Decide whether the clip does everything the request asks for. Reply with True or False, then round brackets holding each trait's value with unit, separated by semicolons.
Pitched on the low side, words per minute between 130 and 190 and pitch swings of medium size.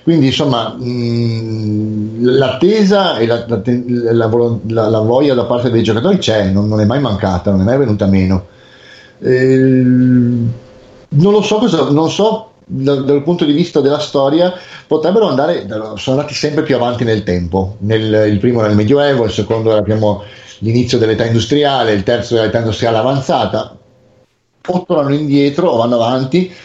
True (120 Hz; 160 wpm; 4.5 semitones)